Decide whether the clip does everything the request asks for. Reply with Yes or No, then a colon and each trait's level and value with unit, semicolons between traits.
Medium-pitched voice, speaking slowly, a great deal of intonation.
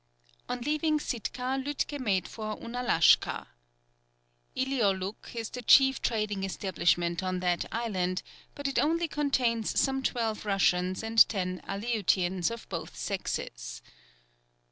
No: high, 220 Hz; slow, 120 wpm; wide, 5.7 semitones